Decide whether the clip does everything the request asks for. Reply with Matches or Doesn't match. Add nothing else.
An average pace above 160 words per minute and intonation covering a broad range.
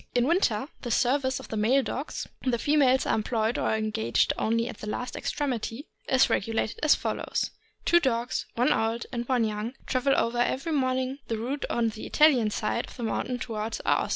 Doesn't match